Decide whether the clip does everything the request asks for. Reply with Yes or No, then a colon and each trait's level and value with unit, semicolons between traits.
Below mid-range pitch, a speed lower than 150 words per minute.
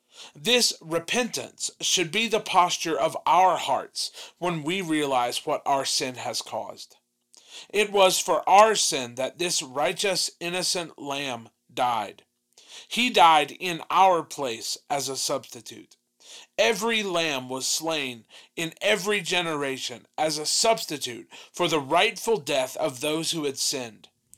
No: medium, 165 Hz; slow, 135 wpm